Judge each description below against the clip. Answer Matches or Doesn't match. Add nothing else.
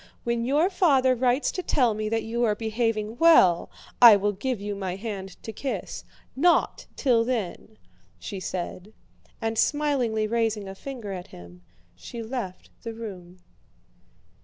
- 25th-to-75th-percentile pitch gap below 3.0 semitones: Doesn't match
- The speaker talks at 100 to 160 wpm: Matches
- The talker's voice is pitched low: Doesn't match